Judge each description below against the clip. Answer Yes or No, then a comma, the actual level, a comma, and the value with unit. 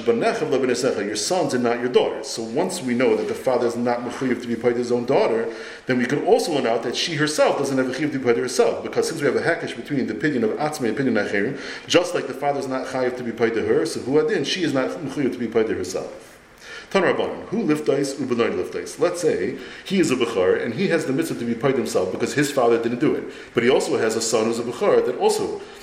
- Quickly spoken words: Yes, fast, 260 wpm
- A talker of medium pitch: Yes, medium, 165 Hz